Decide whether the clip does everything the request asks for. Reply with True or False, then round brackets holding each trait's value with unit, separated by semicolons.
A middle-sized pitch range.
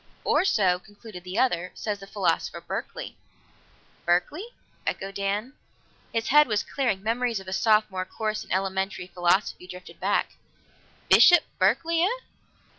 True (4.6 semitones)